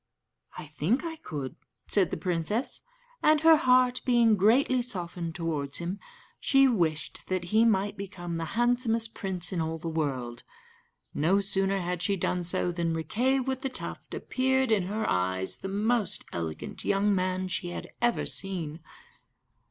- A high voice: Yes, high, 195 Hz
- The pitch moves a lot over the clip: Yes, wide, 5.9 semitones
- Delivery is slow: No, average, 160 wpm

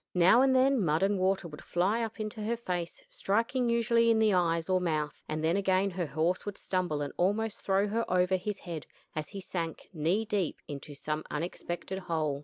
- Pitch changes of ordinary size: Yes, average, 4.4 semitones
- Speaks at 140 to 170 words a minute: No, fast, 205 wpm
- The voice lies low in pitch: No, medium, 185 Hz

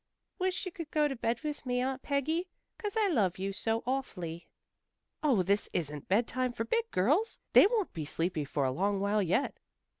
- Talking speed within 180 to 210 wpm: Yes, average, 185 wpm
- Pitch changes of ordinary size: No, wide, 8.4 semitones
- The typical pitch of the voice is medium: No, high, 240 Hz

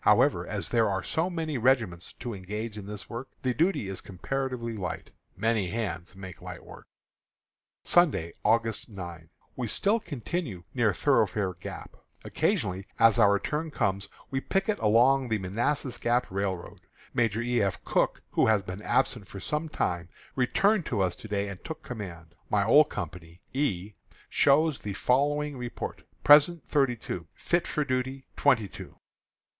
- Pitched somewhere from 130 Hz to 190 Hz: No, low, 115 Hz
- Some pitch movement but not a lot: No, wide, 5.8 semitones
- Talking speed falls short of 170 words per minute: Yes, average, 160 wpm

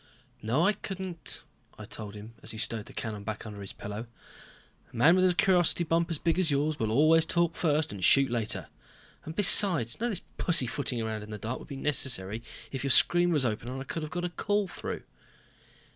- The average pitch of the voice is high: No, medium, 140 Hz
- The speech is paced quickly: Yes, fast, 220 wpm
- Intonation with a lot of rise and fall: Yes, wide, 7.5 semitones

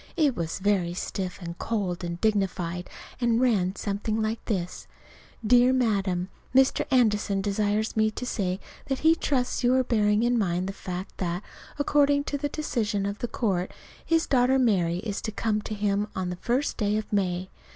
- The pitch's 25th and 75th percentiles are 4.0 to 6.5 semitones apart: Yes, average, 4.6 semitones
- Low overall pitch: No, high, 210 Hz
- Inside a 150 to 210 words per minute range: Yes, average, 180 wpm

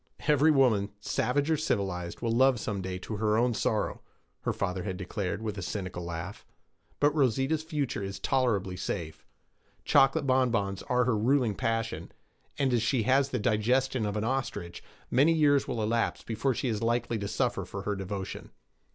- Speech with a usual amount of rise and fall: Yes, average, 4.9 semitones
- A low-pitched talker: Yes, low, 115 Hz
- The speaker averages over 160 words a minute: Yes, average, 175 wpm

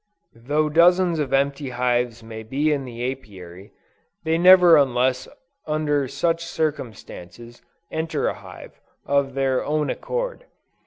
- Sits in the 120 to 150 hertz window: Yes, medium, 140 Hz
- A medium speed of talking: No, slow, 125 wpm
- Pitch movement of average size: Yes, average, 4.4 semitones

